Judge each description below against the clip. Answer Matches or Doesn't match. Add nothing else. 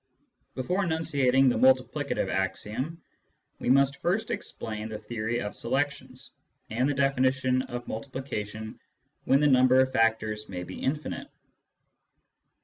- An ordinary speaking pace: Doesn't match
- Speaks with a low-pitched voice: Matches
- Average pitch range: Matches